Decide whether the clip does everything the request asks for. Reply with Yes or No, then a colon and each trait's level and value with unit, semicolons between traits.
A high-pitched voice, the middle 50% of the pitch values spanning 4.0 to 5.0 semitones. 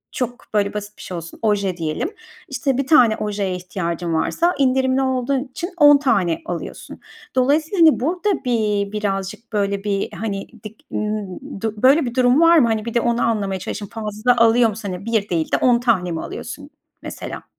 Yes: high, 220 Hz; average, 4.6 semitones